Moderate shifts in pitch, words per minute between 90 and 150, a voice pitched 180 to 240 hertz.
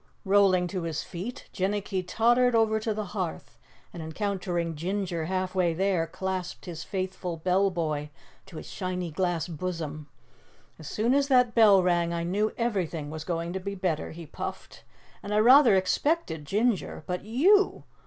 No: average, 3.7 semitones; average, 165 wpm; medium, 185 Hz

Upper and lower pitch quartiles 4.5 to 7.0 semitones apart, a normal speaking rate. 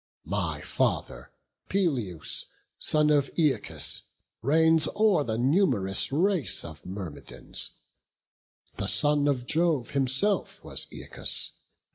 No: wide, 5.6 semitones; slow, 100 wpm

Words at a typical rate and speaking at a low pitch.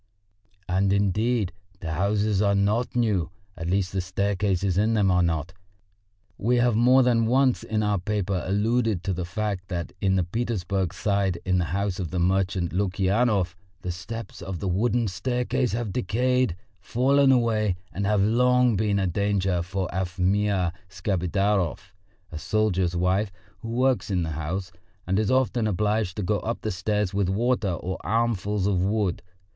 Yes: average, 165 wpm; low, 100 Hz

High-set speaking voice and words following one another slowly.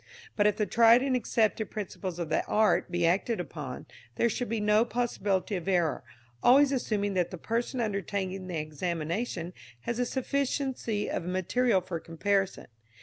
No: high, 205 Hz; average, 160 wpm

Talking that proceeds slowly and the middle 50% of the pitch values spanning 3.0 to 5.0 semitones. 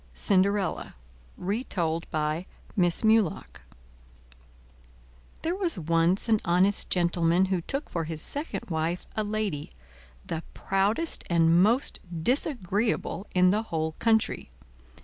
Yes: slow, 110 wpm; average, 4.5 semitones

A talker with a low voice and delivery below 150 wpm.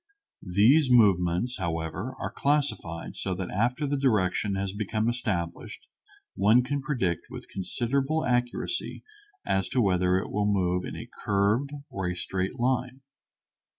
Yes: low, 105 Hz; average, 140 wpm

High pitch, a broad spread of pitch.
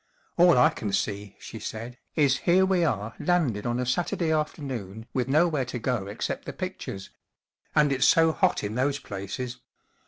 No: low, 130 Hz; wide, 6.2 semitones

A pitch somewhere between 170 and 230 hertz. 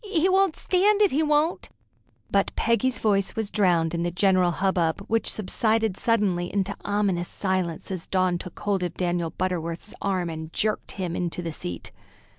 Yes: high, 190 Hz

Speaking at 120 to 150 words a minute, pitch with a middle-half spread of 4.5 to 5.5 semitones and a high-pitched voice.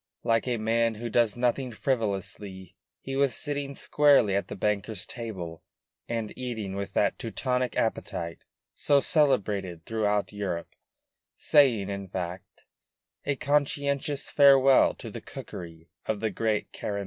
No: slow, 135 wpm; average, 5.1 semitones; low, 110 Hz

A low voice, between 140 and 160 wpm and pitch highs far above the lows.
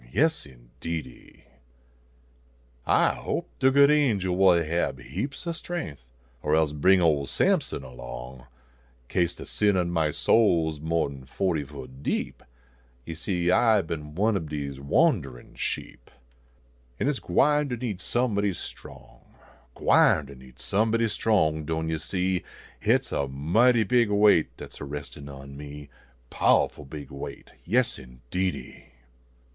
Yes: very low, 80 Hz; average, 150 wpm; wide, 6.9 semitones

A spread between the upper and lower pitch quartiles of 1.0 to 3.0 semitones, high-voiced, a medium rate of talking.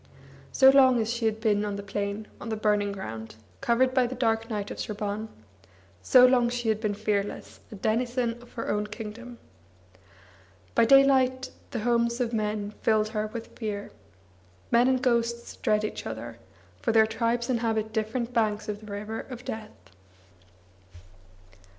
Yes: narrow, 2.4 semitones; high, 225 Hz; average, 160 wpm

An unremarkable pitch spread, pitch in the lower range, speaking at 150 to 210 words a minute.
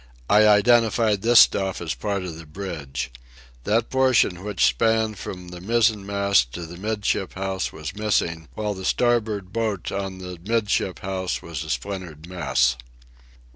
Yes: average, 3.5 semitones; very low, 95 Hz; average, 155 wpm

